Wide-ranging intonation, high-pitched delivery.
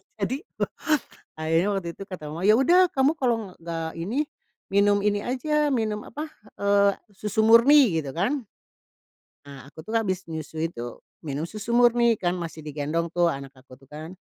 Yes: wide, 6.3 semitones; high, 195 Hz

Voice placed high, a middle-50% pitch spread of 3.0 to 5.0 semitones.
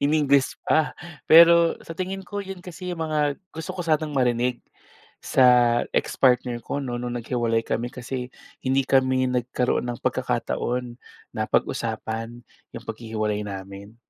No: low, 125 Hz; average, 4.3 semitones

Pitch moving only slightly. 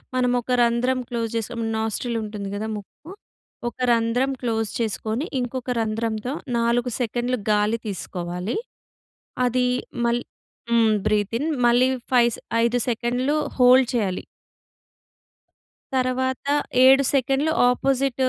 Yes: narrow, 2.3 semitones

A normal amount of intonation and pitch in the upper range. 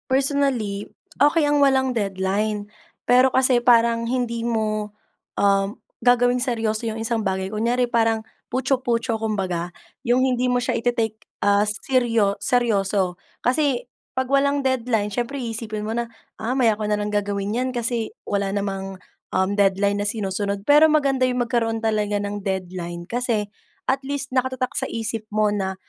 Yes: average, 3.5 semitones; high, 225 Hz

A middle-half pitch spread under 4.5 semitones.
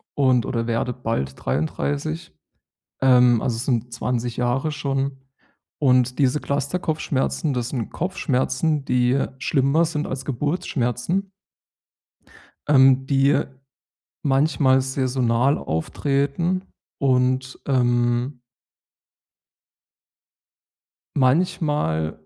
Yes: average, 2.7 semitones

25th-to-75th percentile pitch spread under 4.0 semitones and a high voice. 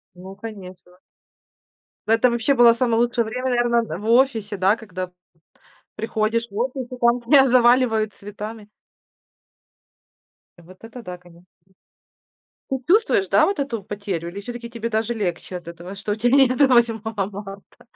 Yes: average, 3.4 semitones; high, 225 Hz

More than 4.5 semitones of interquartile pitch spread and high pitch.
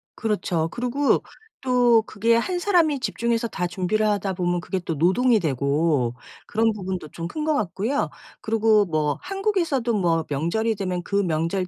Yes: wide, 5.5 semitones; high, 205 Hz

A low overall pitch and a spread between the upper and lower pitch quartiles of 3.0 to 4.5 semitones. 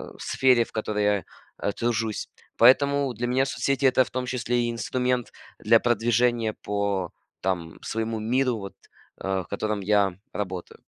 Yes: low, 115 Hz; average, 3.4 semitones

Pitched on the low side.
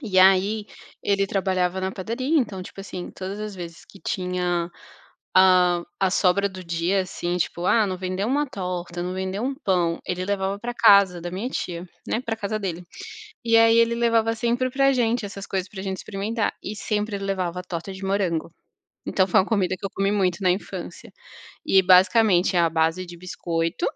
No: high, 190 Hz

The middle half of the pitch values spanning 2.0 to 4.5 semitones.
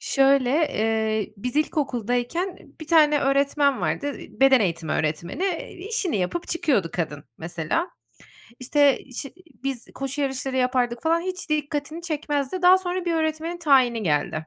No: average, 5.3 semitones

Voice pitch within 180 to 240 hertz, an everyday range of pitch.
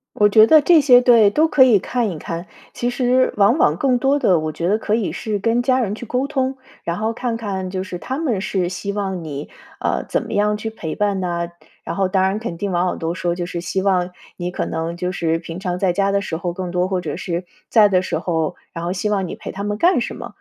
Yes: high, 195 Hz; average, 4.4 semitones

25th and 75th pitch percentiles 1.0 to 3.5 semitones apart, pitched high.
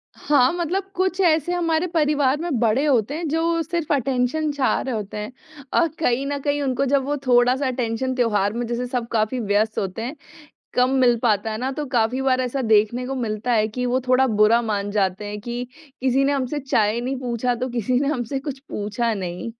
No: average, 3.9 semitones; very high, 250 Hz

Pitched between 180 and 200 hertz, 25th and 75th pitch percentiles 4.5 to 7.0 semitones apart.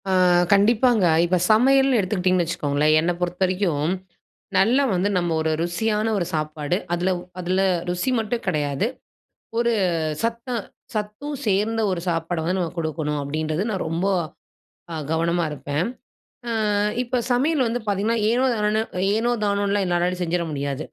Yes: medium, 185 Hz; average, 5.0 semitones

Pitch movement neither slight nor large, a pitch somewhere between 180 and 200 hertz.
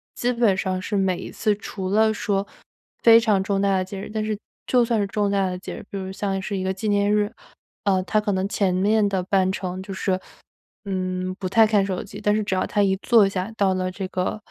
No: narrow, 1.9 semitones; high, 195 Hz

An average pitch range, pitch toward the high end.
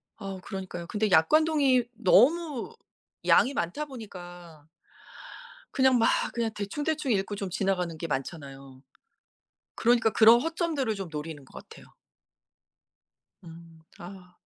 No: wide, 6.9 semitones; high, 200 Hz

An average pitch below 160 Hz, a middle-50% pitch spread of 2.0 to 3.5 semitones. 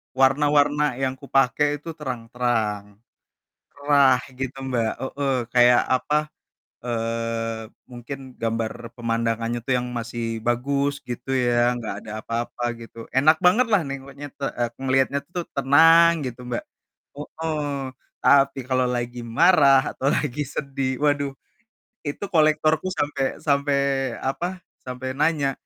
Yes: low, 135 Hz; average, 3.2 semitones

